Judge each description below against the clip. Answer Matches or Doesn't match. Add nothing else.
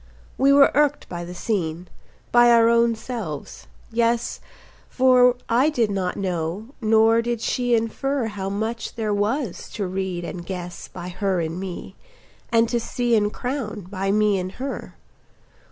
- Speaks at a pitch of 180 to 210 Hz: Doesn't match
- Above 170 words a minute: Doesn't match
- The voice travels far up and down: Doesn't match